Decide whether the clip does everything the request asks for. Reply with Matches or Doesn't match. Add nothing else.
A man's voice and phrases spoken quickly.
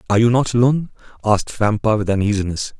Doesn't match